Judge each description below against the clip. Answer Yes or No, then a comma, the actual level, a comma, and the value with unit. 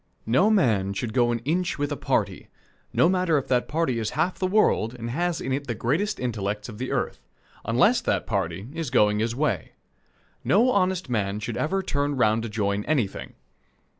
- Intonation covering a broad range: Yes, wide, 7.3 semitones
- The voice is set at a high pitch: No, low, 125 Hz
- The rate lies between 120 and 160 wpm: No, average, 195 wpm